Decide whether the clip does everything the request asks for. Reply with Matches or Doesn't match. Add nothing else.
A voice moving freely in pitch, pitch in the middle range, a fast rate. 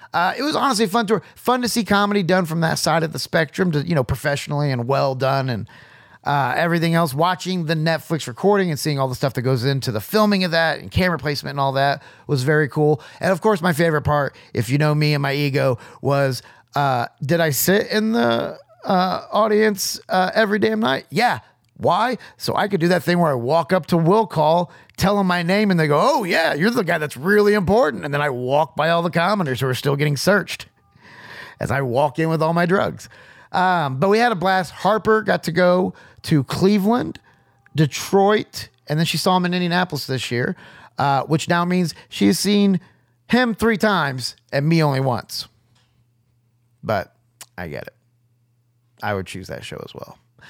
Matches